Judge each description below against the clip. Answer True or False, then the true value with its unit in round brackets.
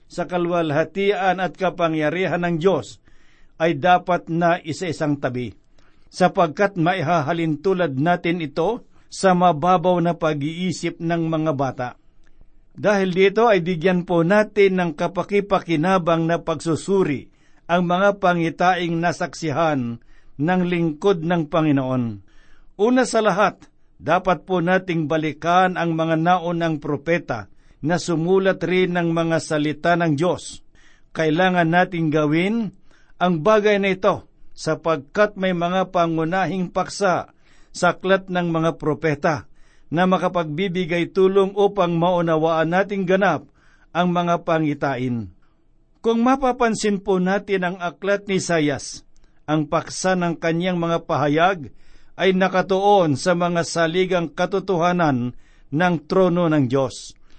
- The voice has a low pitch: False (175 Hz)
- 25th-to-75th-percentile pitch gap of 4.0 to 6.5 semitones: False (2.6 semitones)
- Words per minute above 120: False (115 wpm)